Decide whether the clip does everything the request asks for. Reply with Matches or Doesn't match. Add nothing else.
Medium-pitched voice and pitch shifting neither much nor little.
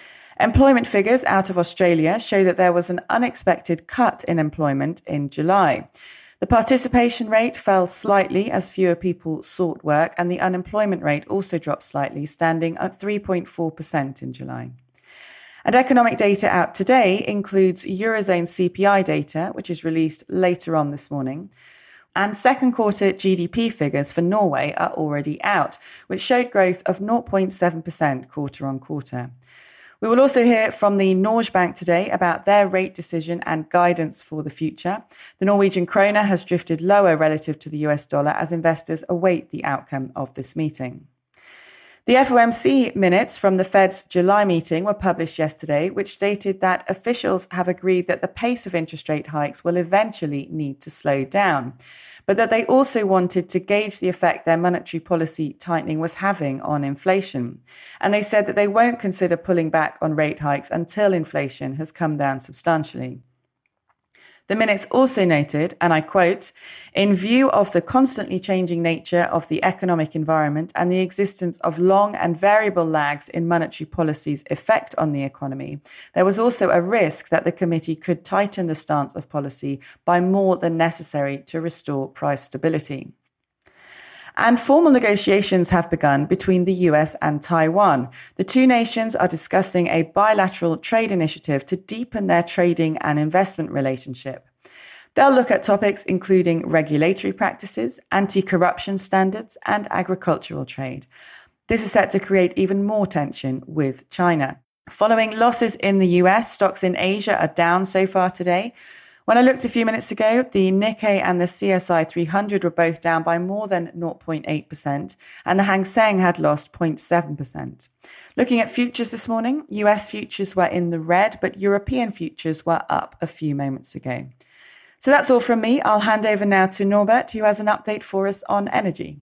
Matches